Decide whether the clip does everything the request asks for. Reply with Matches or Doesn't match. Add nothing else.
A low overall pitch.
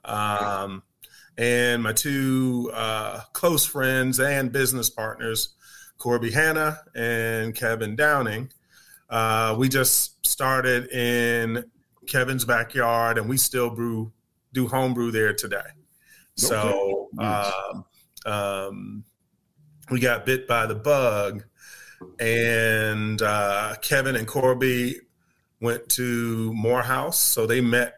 Matches